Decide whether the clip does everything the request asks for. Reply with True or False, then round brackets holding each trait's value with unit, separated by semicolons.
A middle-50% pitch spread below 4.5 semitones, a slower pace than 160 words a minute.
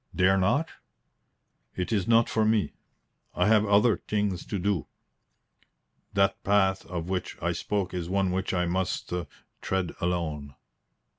True (2.4 semitones; 140 wpm)